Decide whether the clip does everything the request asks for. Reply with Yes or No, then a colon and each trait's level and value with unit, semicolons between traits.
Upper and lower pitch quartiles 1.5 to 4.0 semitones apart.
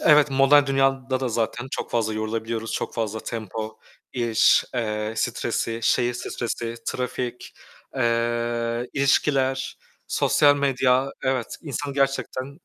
Yes: average, 2.9 semitones